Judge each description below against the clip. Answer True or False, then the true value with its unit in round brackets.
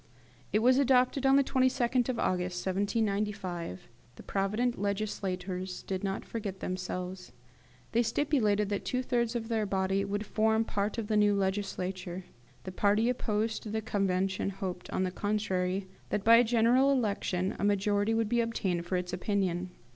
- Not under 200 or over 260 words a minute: False (160 wpm)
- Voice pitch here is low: False (205 Hz)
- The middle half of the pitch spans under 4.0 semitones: True (3.2 semitones)